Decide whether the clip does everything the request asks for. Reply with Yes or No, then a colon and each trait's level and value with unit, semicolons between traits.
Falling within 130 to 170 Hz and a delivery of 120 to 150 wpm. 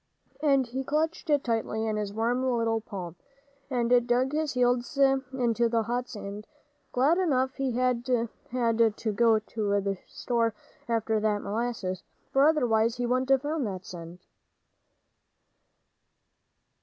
No: high, 240 Hz; average, 140 wpm